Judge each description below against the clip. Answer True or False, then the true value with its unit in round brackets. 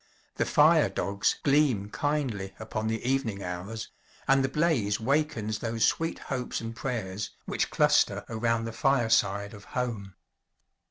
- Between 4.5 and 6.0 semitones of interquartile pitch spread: True (4.8 semitones)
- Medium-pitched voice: False (115 Hz)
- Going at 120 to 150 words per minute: True (140 wpm)